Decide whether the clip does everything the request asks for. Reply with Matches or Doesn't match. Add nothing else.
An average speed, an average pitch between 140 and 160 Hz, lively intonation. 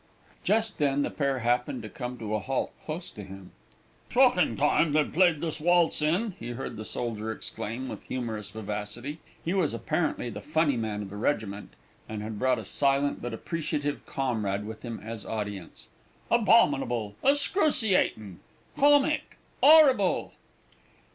Doesn't match